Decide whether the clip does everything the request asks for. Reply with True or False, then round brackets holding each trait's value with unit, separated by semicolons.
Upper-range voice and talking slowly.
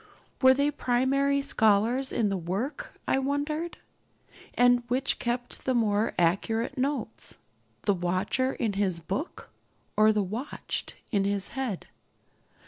True (240 Hz; 130 wpm)